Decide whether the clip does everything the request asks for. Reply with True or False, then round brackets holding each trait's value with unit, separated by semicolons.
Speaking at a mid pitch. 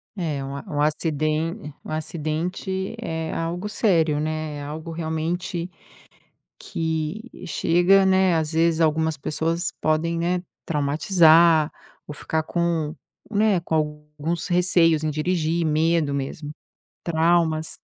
True (160 Hz)